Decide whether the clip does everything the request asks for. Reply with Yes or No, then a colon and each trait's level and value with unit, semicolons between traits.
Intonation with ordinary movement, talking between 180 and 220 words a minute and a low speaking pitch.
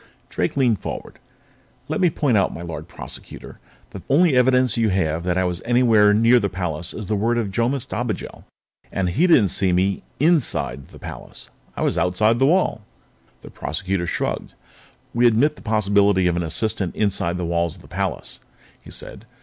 Yes: average, 4.9 semitones; average, 185 wpm; low, 100 Hz